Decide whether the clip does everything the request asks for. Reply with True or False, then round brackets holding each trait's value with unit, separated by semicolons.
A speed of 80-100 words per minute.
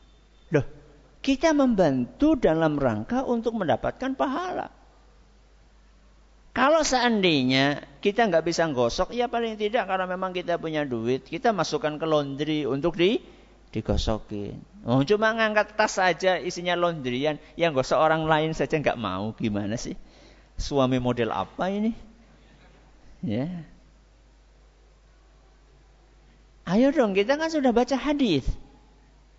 False (115 wpm)